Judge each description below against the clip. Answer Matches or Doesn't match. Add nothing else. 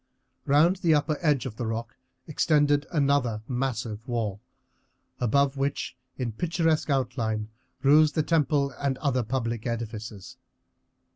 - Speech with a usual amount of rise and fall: Matches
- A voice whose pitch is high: Doesn't match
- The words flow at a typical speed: Doesn't match